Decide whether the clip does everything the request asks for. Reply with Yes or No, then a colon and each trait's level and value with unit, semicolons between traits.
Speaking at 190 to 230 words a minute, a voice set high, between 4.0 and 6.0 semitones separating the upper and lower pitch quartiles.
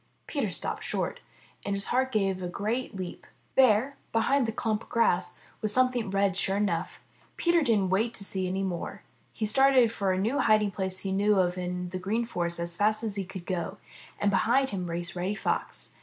No: average, 200 wpm; high, 200 Hz; average, 3.6 semitones